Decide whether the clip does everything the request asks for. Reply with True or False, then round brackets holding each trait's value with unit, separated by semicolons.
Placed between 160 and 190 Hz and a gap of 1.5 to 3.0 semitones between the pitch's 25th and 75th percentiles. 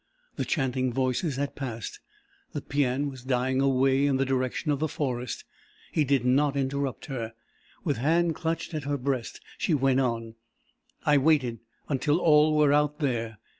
False (135 Hz; 2.5 semitones)